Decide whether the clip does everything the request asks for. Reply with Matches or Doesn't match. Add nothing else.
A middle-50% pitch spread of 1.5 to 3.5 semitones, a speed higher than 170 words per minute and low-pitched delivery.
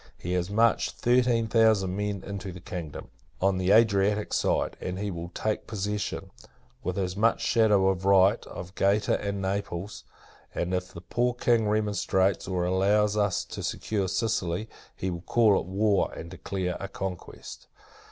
Doesn't match